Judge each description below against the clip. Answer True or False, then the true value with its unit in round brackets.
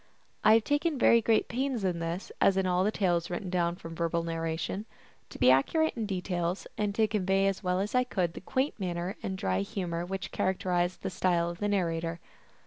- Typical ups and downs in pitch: True (3.3 semitones)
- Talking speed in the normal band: False (210 wpm)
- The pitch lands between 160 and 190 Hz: True (185 Hz)